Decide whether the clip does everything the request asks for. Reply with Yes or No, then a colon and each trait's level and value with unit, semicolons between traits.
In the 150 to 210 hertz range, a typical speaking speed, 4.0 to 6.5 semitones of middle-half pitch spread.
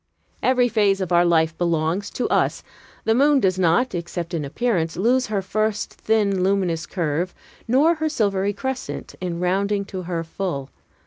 Yes: high, 190 Hz; average, 165 wpm; average, 4.3 semitones